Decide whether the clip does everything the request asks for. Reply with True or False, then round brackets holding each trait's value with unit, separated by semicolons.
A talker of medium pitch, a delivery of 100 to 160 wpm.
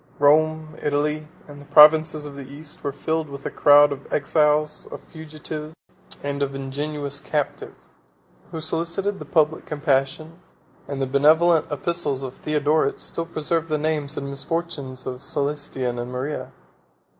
True (150 Hz; 145 wpm)